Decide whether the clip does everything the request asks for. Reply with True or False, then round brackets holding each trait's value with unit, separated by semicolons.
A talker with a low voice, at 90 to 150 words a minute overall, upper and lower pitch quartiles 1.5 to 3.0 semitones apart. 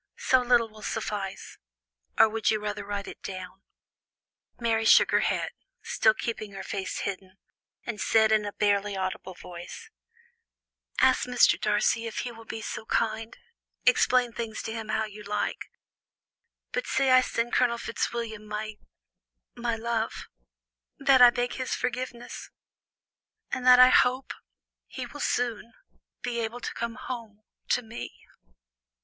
False (225 Hz; 145 wpm; 2.4 semitones)